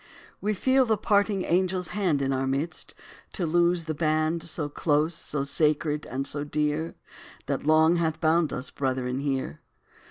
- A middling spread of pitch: Yes, average, 3.2 semitones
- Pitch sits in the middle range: Yes, medium, 155 Hz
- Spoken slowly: No, average, 165 wpm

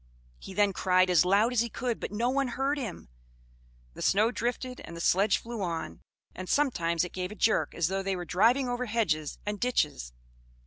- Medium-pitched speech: No, high, 205 Hz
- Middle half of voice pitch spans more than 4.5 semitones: Yes, average, 5.2 semitones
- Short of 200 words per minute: No, fast, 205 wpm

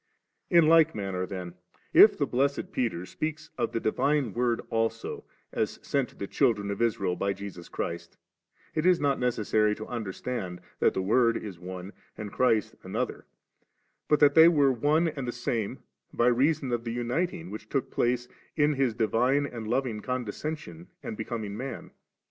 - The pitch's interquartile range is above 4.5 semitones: Yes, average, 4.9 semitones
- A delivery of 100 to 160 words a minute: No, average, 170 wpm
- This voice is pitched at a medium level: No, low, 120 Hz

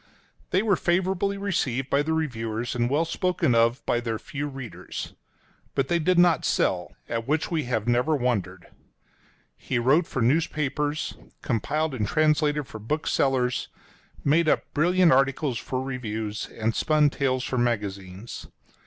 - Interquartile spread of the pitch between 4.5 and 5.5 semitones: Yes, average, 4.8 semitones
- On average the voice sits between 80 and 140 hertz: Yes, low, 135 Hz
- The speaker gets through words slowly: No, average, 150 wpm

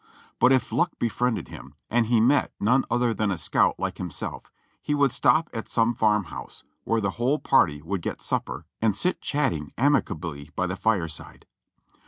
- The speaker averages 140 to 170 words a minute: No, average, 185 wpm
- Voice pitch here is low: Yes, low, 115 Hz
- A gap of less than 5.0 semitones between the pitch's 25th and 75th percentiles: No, average, 5.3 semitones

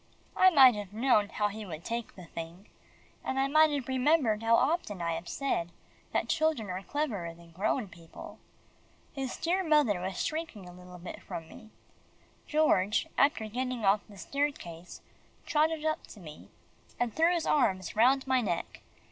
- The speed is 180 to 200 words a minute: No, average, 170 wpm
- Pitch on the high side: Yes, high, 225 Hz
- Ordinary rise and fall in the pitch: No, wide, 7.7 semitones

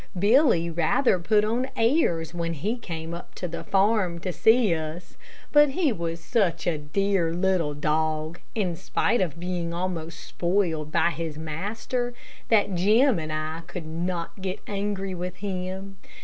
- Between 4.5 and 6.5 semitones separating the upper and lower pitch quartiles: No, average, 3.7 semitones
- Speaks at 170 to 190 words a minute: No, average, 155 wpm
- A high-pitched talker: No, medium, 180 Hz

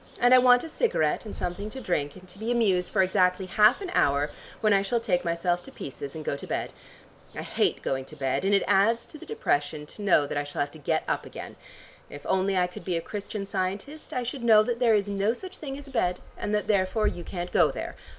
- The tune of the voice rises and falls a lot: No, average, 4.8 semitones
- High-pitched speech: Yes, high, 195 Hz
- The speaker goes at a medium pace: No, fast, 255 wpm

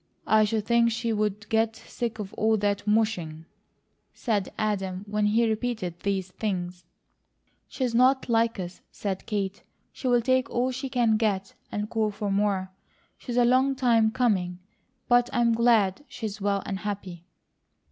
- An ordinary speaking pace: Yes, average, 155 wpm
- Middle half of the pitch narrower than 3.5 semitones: Yes, average, 3.0 semitones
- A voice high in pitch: Yes, high, 215 Hz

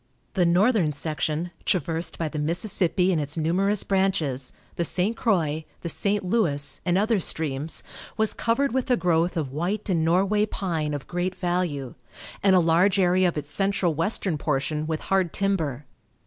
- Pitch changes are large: No, average, 3.9 semitones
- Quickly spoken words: No, average, 165 wpm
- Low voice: No, medium, 175 Hz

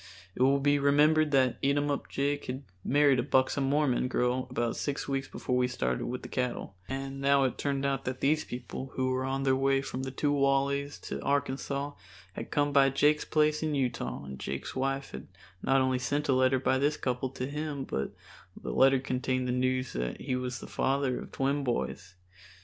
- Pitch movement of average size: No, narrow, 1.7 semitones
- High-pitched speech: No, low, 135 Hz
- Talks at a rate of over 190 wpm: Yes, average, 200 wpm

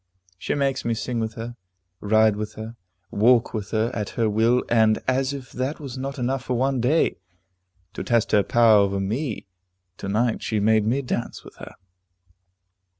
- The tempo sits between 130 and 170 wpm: No, average, 180 wpm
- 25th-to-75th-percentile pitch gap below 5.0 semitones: Yes, average, 2.9 semitones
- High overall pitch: No, low, 115 Hz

